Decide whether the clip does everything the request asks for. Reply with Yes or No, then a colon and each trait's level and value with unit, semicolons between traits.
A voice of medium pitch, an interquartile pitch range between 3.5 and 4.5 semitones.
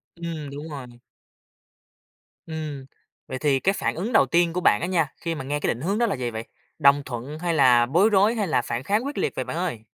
No: medium, 155 Hz; average, 5.0 semitones